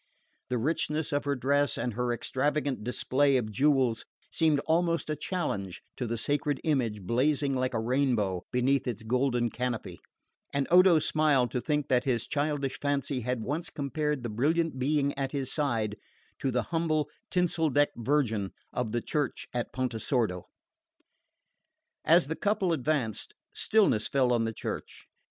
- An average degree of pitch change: Yes, average, 3.8 semitones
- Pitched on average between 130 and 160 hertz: Yes, low, 135 Hz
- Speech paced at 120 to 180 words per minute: Yes, average, 155 wpm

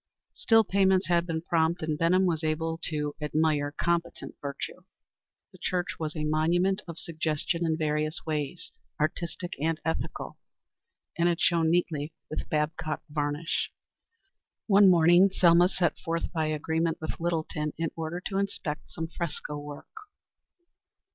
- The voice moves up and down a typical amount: No, narrow, 2.0 semitones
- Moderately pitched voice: Yes, medium, 165 Hz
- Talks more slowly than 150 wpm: Yes, average, 140 wpm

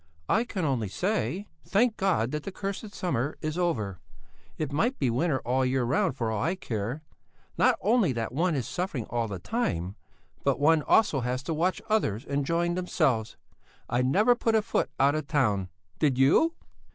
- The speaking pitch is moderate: Yes, medium, 150 Hz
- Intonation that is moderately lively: No, wide, 7.4 semitones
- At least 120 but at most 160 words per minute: No, average, 185 wpm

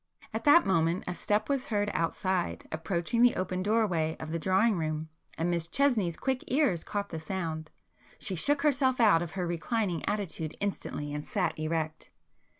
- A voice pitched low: No, medium, 185 Hz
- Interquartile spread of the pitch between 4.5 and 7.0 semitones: Yes, average, 5.3 semitones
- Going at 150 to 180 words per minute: Yes, average, 170 wpm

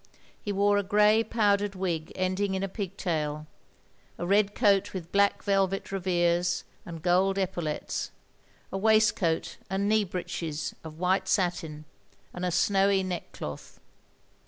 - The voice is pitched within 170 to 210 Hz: Yes, high, 190 Hz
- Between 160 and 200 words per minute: No, average, 140 wpm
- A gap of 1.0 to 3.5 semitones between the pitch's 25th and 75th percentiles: Yes, narrow, 2.6 semitones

